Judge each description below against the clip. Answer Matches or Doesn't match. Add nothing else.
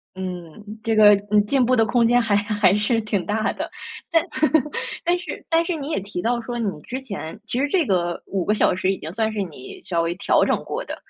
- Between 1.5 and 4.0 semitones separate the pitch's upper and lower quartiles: Doesn't match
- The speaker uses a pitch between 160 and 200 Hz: Doesn't match